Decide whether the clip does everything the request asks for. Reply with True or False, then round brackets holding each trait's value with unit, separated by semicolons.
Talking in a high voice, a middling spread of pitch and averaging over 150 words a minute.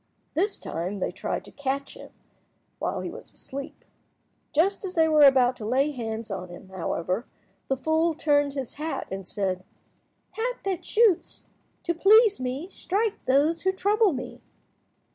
False (290 Hz; 6.9 semitones; 160 wpm)